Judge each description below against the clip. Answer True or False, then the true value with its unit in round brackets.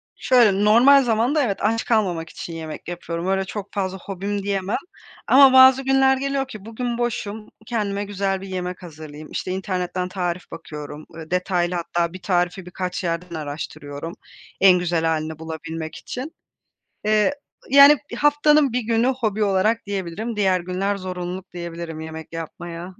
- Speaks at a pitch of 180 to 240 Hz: True (190 Hz)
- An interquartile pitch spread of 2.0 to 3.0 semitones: False (4.5 semitones)